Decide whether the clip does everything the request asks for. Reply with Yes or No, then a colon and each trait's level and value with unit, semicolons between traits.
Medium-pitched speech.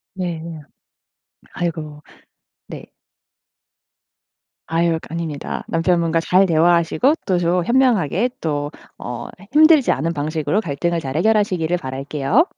Yes: medium, 170 Hz